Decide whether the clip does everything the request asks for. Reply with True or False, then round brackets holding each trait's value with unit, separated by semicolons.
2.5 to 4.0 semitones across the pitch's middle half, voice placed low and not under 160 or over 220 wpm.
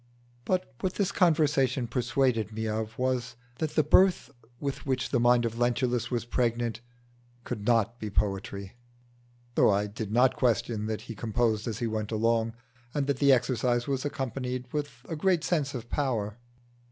True (3.3 semitones; 120 Hz; 165 wpm)